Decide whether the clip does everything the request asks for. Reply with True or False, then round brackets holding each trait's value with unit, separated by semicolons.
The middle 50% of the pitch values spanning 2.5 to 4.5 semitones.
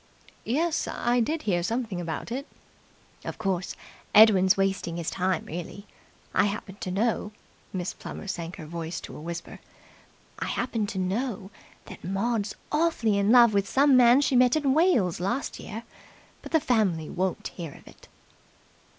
False (5.0 semitones)